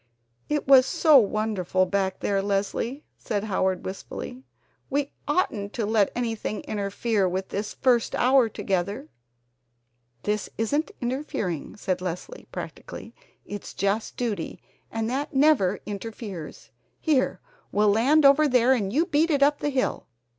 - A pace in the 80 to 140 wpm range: Yes, slow, 135 wpm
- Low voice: No, high, 220 Hz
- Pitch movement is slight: No, average, 5.3 semitones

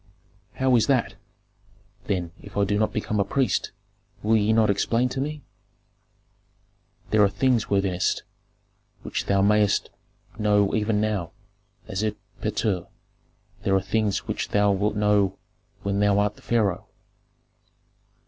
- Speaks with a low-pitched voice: Yes, low, 105 Hz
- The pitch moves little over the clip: Yes, narrow, 1.6 semitones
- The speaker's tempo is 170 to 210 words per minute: No, slow, 135 wpm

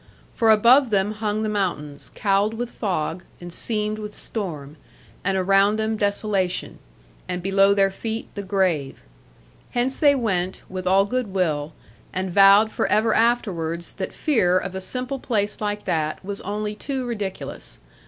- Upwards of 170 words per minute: No, average, 155 wpm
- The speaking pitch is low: No, high, 200 Hz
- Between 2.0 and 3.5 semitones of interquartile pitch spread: Yes, average, 2.8 semitones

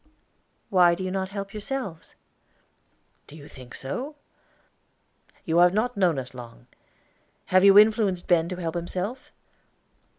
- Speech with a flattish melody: No, average, 3.8 semitones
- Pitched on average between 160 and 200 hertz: Yes, medium, 185 Hz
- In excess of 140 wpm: No, slow, 135 wpm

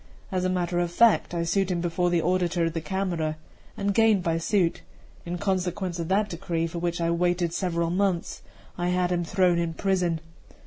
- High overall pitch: No, medium, 175 Hz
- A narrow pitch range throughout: Yes, narrow, 1.8 semitones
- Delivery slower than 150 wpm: No, average, 195 wpm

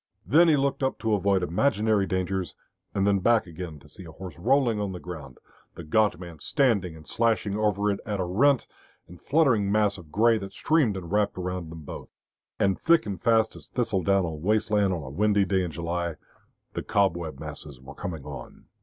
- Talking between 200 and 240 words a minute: Yes, fast, 205 wpm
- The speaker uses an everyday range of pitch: Yes, average, 3.9 semitones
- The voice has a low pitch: Yes, very low, 95 Hz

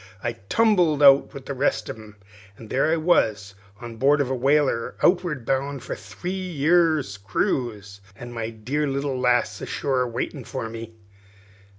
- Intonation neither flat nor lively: Yes, average, 4.6 semitones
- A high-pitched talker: No, low, 130 Hz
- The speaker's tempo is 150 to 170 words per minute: Yes, average, 160 wpm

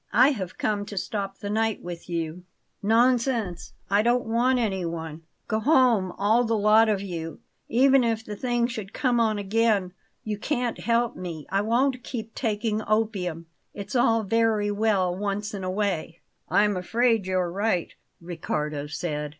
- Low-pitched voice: No, high, 210 Hz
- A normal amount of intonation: Yes, average, 3.8 semitones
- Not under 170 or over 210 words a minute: No, average, 160 wpm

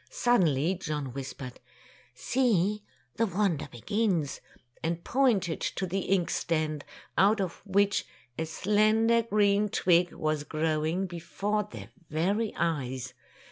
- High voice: No, medium, 180 Hz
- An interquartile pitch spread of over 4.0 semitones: Yes, average, 5.0 semitones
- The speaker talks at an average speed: No, slow, 115 wpm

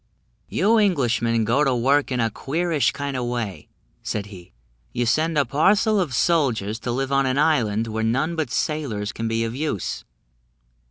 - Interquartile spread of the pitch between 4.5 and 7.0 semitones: Yes, average, 5.1 semitones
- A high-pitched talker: No, low, 130 Hz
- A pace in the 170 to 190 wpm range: Yes, average, 175 wpm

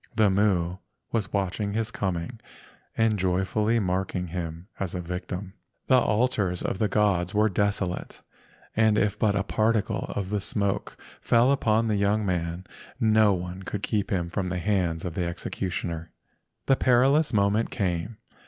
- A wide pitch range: No, average, 3.1 semitones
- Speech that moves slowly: No, average, 155 wpm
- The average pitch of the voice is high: No, low, 100 Hz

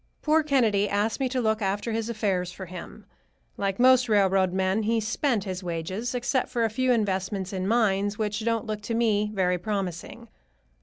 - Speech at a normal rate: Yes, average, 185 wpm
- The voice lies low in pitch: No, high, 210 Hz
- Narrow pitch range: No, average, 3.3 semitones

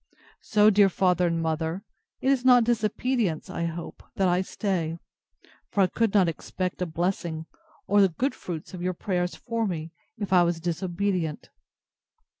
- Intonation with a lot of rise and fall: No, average, 3.4 semitones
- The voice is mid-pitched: Yes, medium, 180 Hz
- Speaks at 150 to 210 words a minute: Yes, average, 165 wpm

